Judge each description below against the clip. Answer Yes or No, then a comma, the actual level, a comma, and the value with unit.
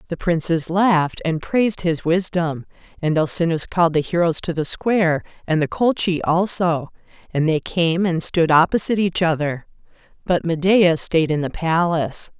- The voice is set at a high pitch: No, medium, 170 Hz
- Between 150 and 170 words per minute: Yes, average, 160 wpm